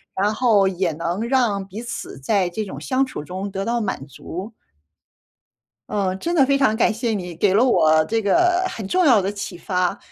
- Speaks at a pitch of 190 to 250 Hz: Yes, high, 205 Hz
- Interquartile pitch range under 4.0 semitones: No, average, 4.3 semitones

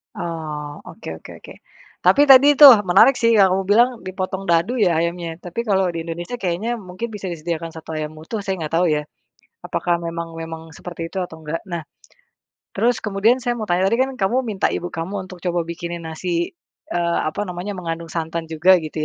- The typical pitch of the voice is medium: Yes, medium, 175 Hz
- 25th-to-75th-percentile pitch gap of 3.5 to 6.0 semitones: No, average, 2.9 semitones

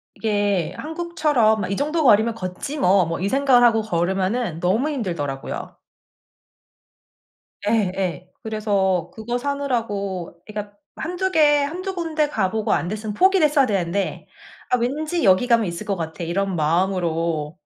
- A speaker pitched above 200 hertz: Yes, high, 210 Hz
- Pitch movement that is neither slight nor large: No, wide, 7.3 semitones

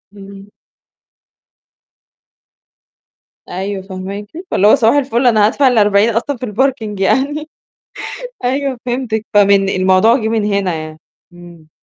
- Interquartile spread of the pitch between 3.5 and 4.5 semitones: Yes, average, 4.0 semitones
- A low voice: No, high, 210 Hz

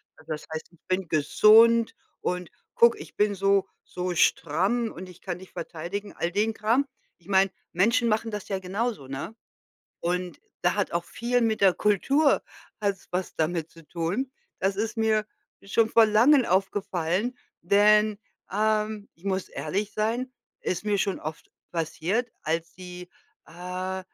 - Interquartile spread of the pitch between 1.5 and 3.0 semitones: No, average, 3.5 semitones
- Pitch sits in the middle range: No, high, 195 Hz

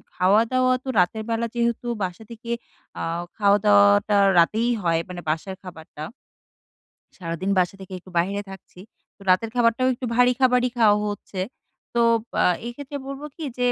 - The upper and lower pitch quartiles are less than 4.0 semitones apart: No, average, 4.5 semitones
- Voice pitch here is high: Yes, high, 210 Hz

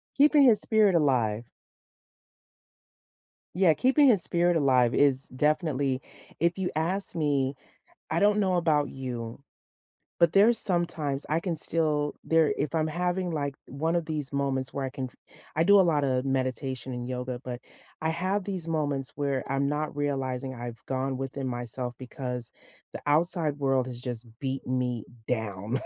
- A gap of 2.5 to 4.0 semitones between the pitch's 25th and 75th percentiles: No, average, 4.5 semitones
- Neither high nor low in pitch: Yes, medium, 145 Hz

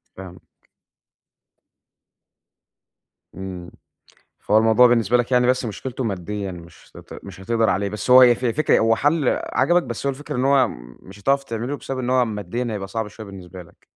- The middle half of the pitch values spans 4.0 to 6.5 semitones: Yes, average, 4.5 semitones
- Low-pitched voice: Yes, low, 115 Hz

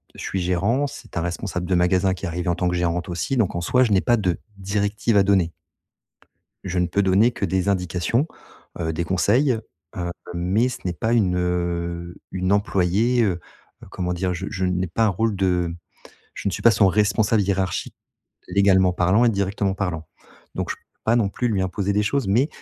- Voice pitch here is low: Yes, very low, 95 Hz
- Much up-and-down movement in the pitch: No, average, 2.9 semitones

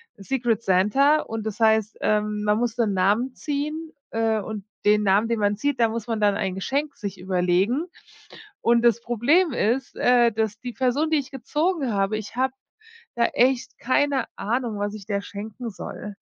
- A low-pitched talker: No, high, 225 Hz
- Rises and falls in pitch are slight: No, average, 3.7 semitones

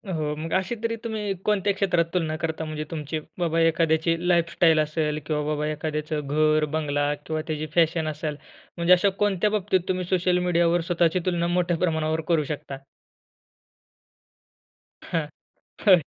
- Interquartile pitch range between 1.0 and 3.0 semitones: Yes, narrow, 2.6 semitones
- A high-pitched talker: No, medium, 165 Hz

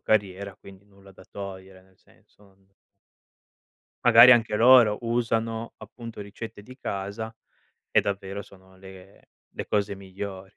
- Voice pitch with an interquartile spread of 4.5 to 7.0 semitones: No, average, 2.7 semitones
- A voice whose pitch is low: Yes, low, 100 Hz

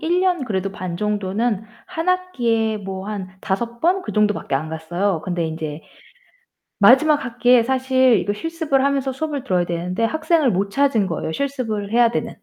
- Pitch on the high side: Yes, high, 225 Hz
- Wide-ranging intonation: Yes, wide, 6.4 semitones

